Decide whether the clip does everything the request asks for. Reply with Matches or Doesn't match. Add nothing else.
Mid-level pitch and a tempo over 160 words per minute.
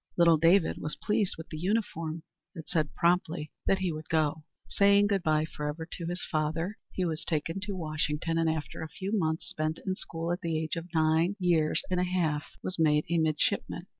Matches